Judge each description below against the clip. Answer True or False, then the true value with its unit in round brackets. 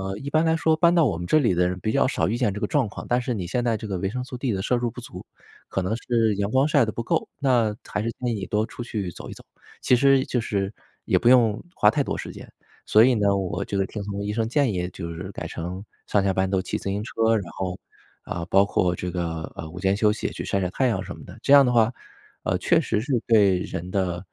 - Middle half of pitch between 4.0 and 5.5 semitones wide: True (4.4 semitones)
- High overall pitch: False (105 Hz)